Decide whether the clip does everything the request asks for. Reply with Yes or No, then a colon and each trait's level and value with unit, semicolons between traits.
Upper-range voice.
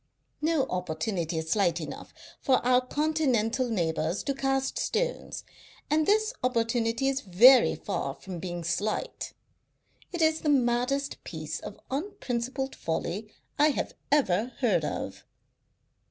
Yes: high, 245 Hz